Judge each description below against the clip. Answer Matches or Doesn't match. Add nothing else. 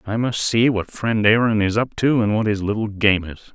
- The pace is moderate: Doesn't match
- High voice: Doesn't match